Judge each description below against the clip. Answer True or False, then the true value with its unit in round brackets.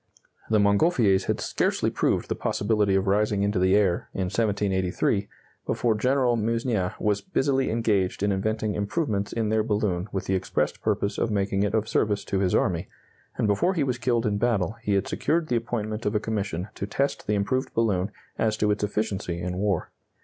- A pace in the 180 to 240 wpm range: True (190 wpm)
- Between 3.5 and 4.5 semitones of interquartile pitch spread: False (2.5 semitones)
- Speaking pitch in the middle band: False (105 Hz)